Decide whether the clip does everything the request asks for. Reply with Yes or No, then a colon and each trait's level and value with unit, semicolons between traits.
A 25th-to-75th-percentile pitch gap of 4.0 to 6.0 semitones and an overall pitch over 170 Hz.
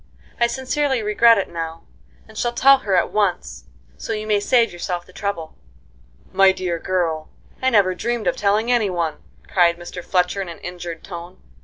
Yes: average, 4.4 semitones; high, 190 Hz